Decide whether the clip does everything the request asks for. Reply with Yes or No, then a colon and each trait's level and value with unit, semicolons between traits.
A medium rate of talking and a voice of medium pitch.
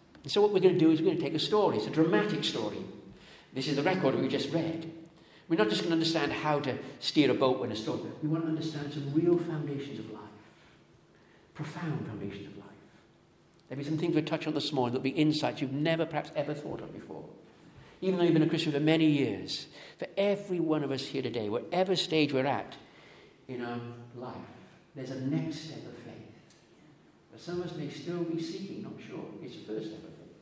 No: fast, 225 wpm; medium, 150 Hz